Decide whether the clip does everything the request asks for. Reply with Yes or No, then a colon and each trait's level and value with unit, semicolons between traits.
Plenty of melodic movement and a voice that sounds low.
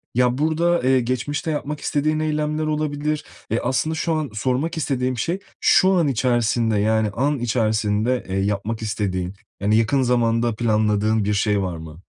Yes: wide, 5.7 semitones; low, 120 Hz